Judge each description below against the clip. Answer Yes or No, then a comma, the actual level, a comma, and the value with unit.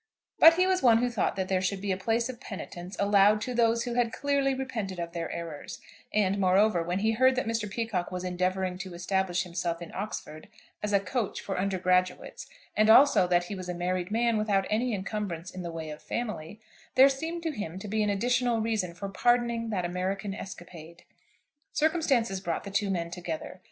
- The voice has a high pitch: Yes, high, 200 Hz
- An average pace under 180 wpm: No, average, 200 wpm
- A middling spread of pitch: Yes, average, 4.2 semitones